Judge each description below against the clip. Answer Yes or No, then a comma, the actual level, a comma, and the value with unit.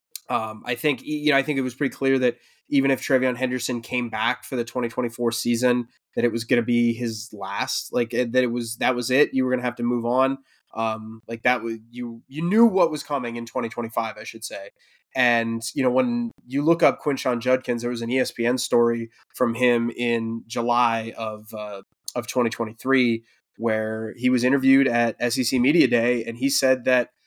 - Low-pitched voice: Yes, low, 120 Hz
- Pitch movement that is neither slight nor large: No, narrow, 1.8 semitones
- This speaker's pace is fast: Yes, fast, 220 wpm